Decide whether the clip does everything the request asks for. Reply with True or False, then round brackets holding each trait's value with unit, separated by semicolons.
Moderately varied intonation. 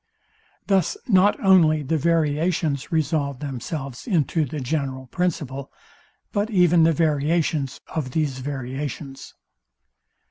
True (3.6 semitones)